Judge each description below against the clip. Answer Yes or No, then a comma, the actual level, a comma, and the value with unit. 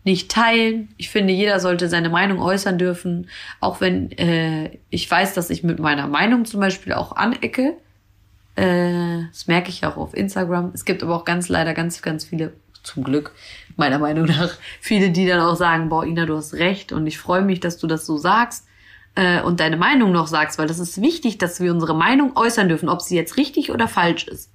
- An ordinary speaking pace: No, fast, 215 wpm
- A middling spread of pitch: Yes, average, 3.0 semitones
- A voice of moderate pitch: Yes, medium, 175 Hz